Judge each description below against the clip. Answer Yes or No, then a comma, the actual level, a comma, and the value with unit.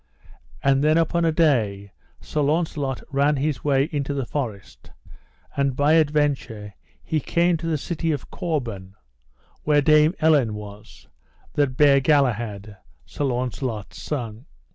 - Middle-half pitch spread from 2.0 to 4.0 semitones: No, average, 4.5 semitones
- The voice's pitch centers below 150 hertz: Yes, medium, 140 Hz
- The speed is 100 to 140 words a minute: Yes, slow, 135 wpm